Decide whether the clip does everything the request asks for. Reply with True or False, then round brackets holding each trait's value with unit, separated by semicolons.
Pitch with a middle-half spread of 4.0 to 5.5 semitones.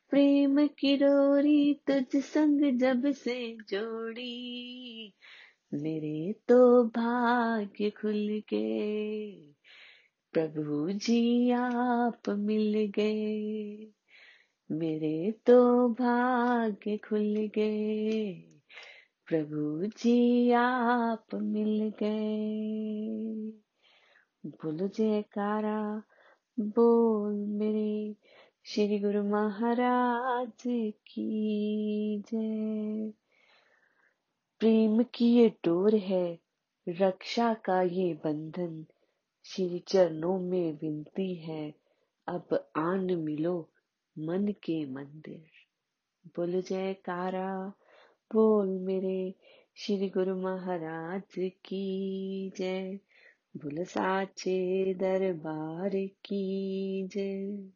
False (3.6 semitones)